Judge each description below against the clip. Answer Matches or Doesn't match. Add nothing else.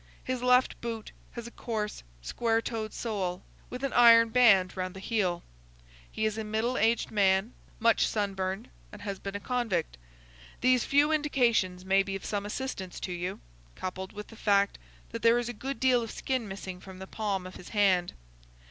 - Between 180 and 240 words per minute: Matches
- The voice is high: Matches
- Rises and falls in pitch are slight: Doesn't match